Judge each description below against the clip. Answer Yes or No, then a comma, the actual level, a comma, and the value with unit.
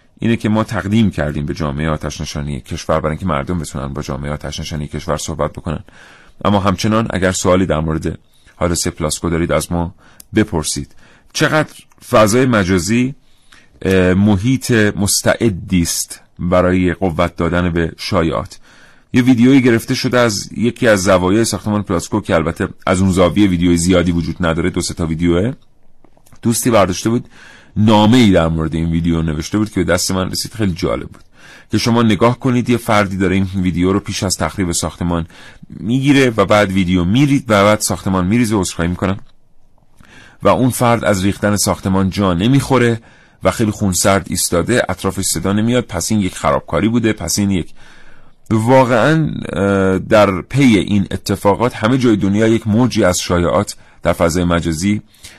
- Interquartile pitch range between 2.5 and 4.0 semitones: No, average, 4.5 semitones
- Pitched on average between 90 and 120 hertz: Yes, very low, 95 Hz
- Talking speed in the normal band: No, fast, 160 wpm